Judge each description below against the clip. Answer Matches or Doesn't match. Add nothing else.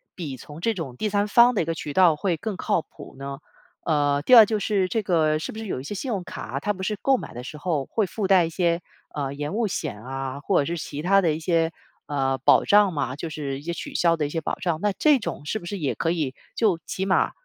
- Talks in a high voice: Doesn't match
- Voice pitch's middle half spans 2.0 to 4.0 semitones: Doesn't match